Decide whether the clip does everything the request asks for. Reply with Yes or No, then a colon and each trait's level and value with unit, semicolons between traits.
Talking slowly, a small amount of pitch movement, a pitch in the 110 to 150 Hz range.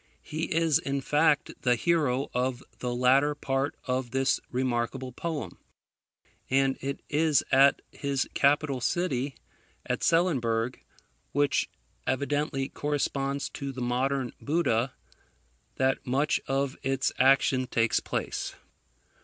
Yes: slow, 110 wpm; narrow, 2.2 semitones; low, 135 Hz